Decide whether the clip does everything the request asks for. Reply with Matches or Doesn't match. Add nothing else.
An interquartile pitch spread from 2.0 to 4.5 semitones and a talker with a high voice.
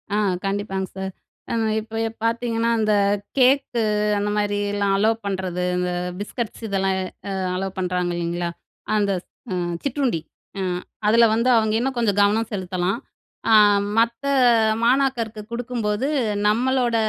Matches